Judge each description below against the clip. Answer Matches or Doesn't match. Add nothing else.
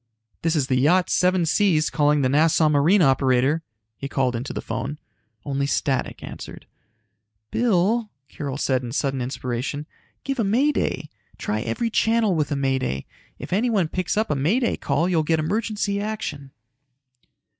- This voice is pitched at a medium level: Matches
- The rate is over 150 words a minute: Matches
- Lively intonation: Matches